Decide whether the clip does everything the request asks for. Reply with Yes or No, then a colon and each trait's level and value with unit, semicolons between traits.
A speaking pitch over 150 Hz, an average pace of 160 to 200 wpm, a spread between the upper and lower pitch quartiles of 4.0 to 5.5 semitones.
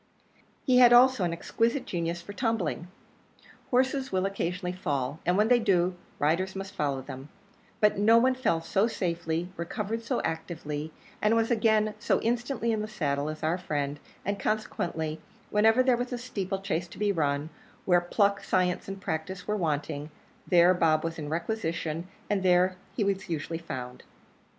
Yes: medium, 185 Hz; average, 170 wpm; average, 5.1 semitones